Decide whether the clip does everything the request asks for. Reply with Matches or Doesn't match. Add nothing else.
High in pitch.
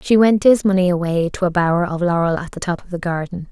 Doesn't match